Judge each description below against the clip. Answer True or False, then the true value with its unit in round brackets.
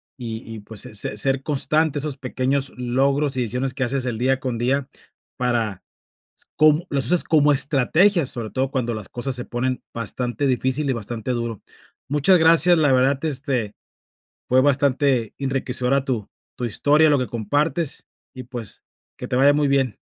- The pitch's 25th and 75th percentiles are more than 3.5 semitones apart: False (2.8 semitones)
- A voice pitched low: True (130 Hz)